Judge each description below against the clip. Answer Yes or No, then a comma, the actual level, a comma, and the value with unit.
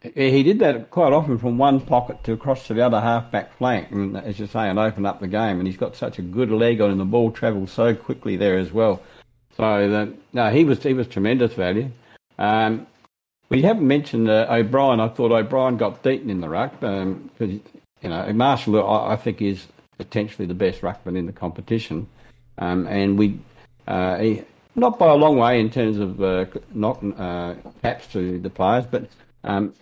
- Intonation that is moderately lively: Yes, average, 3.3 semitones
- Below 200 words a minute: No, fast, 205 wpm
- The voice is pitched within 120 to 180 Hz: No, low, 110 Hz